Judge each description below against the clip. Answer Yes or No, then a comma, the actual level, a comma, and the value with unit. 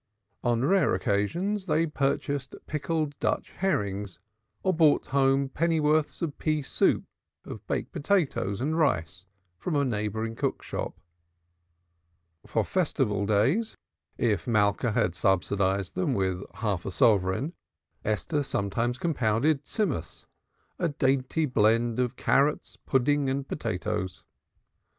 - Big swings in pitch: Yes, wide, 6.8 semitones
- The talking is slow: Yes, slow, 120 wpm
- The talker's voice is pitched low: Yes, low, 130 Hz